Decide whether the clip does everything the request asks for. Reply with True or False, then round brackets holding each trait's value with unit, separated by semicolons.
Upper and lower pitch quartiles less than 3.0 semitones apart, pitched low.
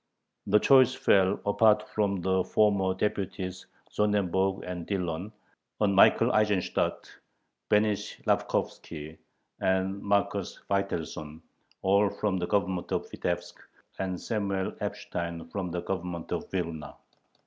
True (2.5 semitones; 95 Hz)